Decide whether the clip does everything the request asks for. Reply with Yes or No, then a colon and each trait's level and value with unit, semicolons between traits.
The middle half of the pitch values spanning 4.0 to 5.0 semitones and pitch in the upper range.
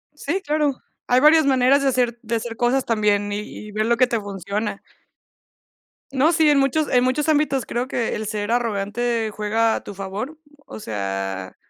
Yes: average, 4.5 semitones; high, 235 Hz